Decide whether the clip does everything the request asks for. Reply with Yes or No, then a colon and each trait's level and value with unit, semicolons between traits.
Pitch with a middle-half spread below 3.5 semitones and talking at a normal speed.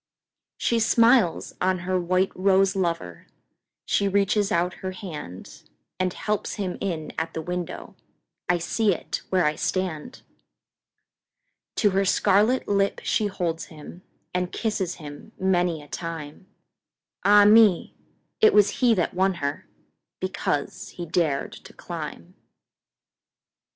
No: average, 3.1 semitones; slow, 110 wpm